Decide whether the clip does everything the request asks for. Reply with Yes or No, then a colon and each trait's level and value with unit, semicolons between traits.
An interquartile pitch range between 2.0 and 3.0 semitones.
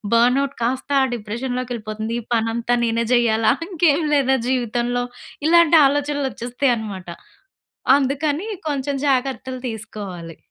No: average, 3.5 semitones